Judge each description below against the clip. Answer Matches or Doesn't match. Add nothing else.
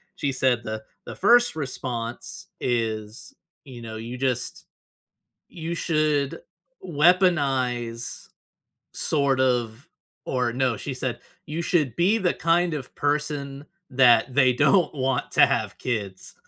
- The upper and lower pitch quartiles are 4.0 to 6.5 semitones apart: Matches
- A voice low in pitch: Matches